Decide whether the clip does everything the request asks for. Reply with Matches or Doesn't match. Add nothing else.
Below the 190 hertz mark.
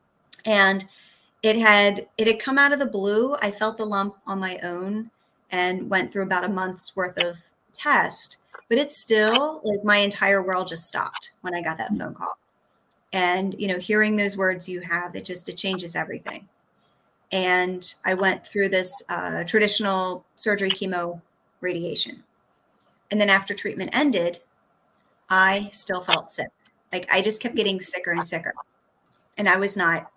Doesn't match